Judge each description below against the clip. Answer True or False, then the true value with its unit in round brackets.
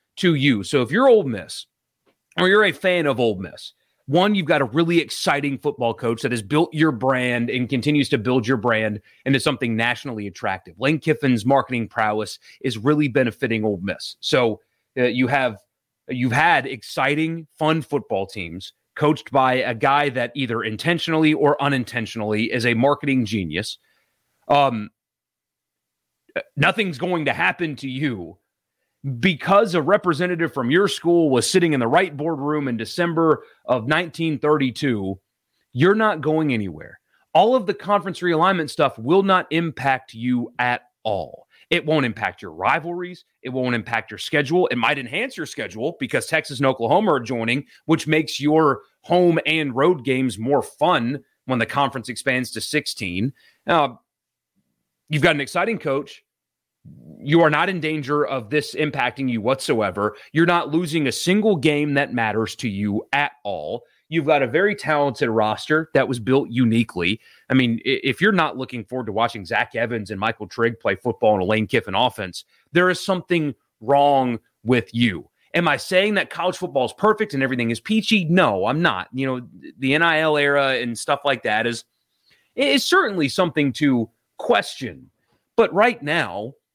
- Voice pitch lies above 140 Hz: False (135 Hz)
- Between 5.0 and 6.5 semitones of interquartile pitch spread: True (5.4 semitones)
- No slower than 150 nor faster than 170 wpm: True (165 wpm)